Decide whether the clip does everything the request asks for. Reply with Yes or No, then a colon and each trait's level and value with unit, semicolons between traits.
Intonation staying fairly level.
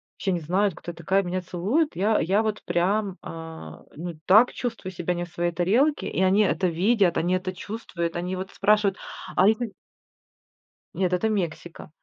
No: average, 3.2 semitones